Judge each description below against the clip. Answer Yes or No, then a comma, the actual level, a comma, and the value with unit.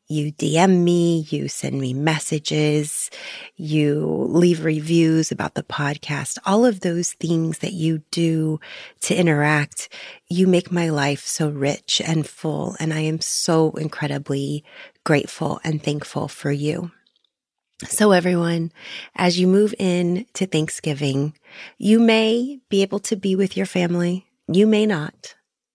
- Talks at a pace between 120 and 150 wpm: Yes, average, 140 wpm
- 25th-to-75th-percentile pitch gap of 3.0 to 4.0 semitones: Yes, average, 3.4 semitones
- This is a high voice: No, medium, 165 Hz